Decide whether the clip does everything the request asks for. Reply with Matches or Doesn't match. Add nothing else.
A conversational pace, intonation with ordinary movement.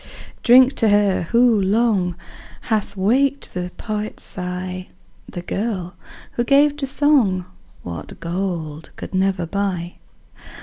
Doesn't match